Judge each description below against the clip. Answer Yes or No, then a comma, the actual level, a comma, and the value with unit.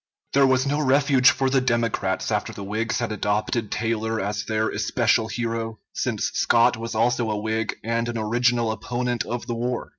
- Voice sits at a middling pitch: No, low, 115 Hz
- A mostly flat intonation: Yes, narrow, 1.8 semitones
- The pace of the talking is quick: No, average, 180 wpm